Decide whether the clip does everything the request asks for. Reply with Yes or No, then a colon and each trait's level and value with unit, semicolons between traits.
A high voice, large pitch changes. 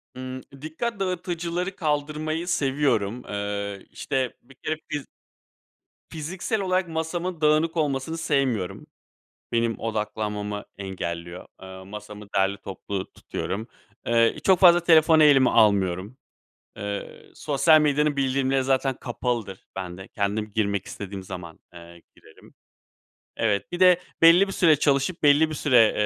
No: low, 130 Hz; wide, 7.5 semitones